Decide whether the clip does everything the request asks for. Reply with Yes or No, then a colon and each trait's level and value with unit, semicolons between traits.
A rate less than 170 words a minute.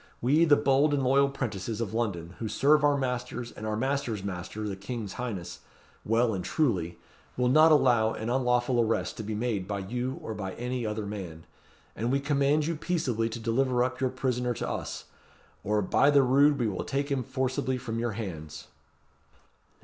No: average, 190 wpm